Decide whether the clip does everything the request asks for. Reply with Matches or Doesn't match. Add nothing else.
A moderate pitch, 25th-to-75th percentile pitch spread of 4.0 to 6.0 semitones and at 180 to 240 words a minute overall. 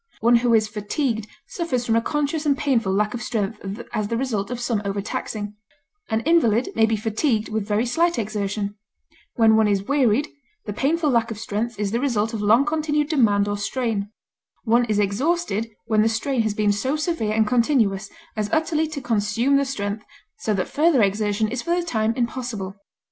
Doesn't match